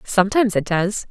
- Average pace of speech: Yes, average, 160 wpm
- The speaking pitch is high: Yes, high, 200 Hz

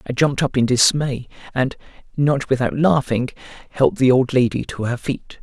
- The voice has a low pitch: Yes, low, 130 Hz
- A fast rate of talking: No, average, 175 wpm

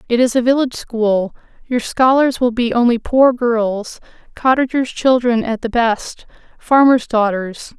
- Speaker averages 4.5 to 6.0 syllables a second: No, 4.2 syllables/s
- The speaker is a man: No, female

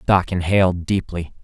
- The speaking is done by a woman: No, male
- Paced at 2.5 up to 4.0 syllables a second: No, 4.8 syllables/s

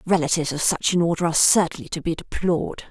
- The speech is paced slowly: No, fast, 205 wpm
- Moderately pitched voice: Yes, medium, 165 Hz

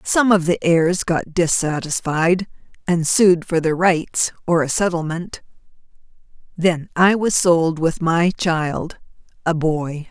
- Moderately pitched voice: Yes, medium, 170 Hz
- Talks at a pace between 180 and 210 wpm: No, slow, 135 wpm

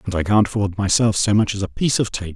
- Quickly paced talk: Yes, fast, 305 wpm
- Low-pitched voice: Yes, low, 105 Hz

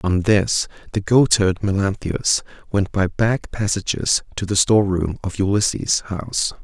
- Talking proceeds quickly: No, average, 145 wpm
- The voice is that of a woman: No, male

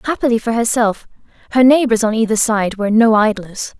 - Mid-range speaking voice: No, high, 225 Hz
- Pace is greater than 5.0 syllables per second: Yes, 5.7 syllables/s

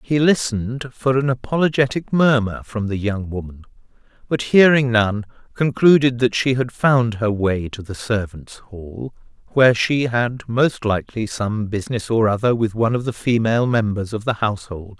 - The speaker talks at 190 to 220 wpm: No, average, 170 wpm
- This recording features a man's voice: Yes, male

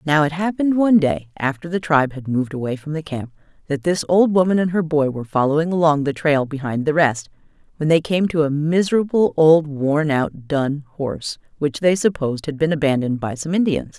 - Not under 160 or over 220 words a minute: Yes, fast, 205 wpm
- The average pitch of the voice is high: No, medium, 155 Hz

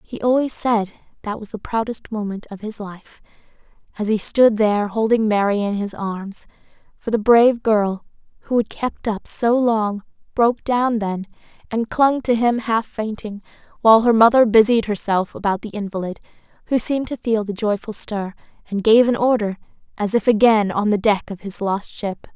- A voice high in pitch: Yes, high, 215 Hz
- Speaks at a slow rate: No, average, 185 wpm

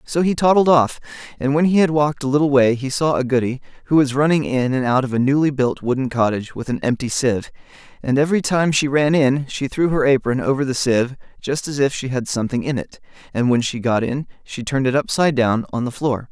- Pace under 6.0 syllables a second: No, 6.1 syllables/s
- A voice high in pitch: No, low, 135 Hz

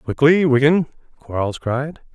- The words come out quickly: No, slow, 110 wpm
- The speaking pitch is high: No, medium, 140 Hz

